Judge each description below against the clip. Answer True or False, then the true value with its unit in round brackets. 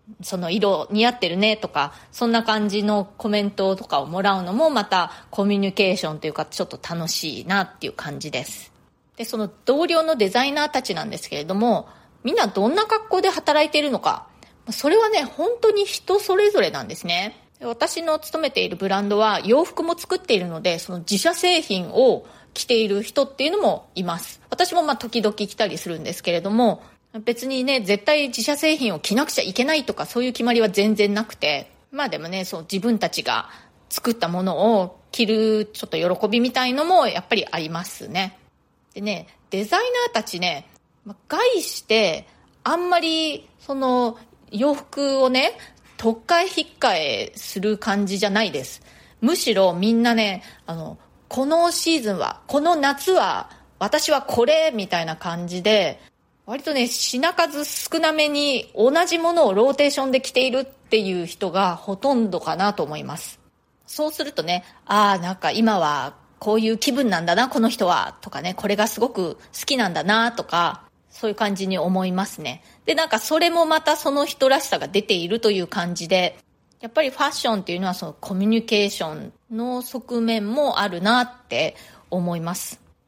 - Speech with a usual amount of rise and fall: False (6.8 semitones)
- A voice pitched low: False (225 Hz)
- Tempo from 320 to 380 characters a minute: True (350 characters per minute)